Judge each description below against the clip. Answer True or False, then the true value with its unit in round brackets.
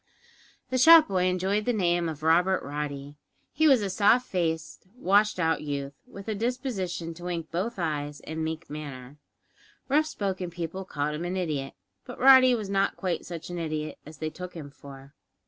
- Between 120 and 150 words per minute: False (185 wpm)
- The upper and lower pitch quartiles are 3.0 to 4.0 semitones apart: False (4.6 semitones)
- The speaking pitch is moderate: True (175 Hz)